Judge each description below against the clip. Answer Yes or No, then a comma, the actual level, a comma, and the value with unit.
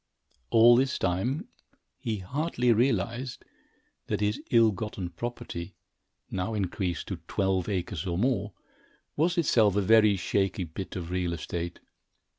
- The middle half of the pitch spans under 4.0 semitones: No, average, 4.6 semitones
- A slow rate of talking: Yes, slow, 130 wpm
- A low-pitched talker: Yes, low, 105 Hz